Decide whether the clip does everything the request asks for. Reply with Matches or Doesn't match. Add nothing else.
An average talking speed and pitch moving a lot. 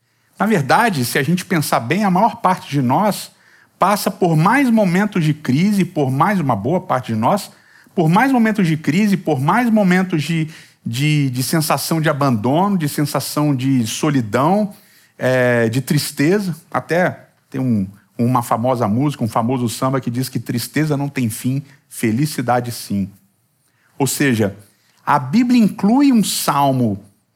Matches